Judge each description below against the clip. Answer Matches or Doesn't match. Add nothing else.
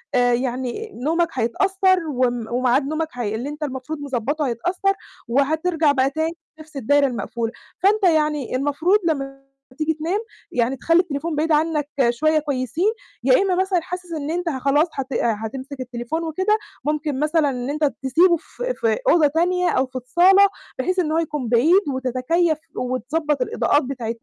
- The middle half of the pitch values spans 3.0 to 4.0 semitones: Doesn't match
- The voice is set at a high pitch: Matches